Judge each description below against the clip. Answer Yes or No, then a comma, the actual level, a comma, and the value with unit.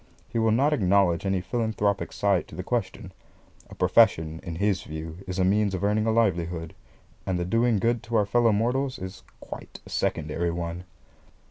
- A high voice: No, low, 100 Hz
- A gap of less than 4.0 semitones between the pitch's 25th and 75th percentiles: No, average, 4.3 semitones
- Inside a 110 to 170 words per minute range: No, average, 180 wpm